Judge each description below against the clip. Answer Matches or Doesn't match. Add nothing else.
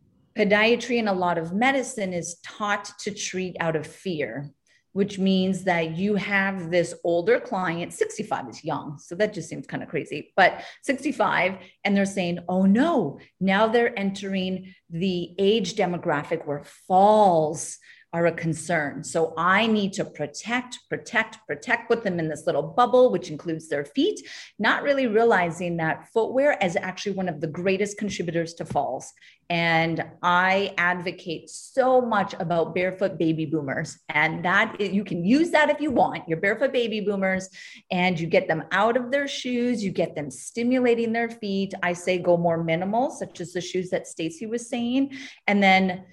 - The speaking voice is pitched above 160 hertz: Matches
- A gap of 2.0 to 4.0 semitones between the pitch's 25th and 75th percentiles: Doesn't match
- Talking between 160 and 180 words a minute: Matches